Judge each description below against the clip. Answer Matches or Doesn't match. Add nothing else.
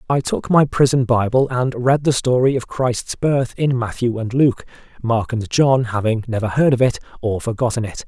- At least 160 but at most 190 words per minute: Doesn't match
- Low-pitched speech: Matches